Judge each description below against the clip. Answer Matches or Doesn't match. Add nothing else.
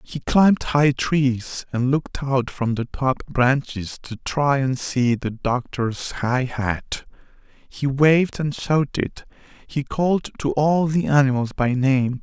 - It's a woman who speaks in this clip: Doesn't match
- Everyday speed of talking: Matches